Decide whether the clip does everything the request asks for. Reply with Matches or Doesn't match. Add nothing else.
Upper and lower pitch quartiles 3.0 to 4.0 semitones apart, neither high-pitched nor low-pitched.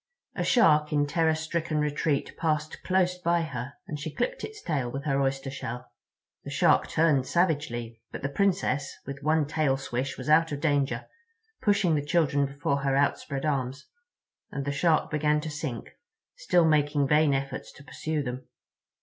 Doesn't match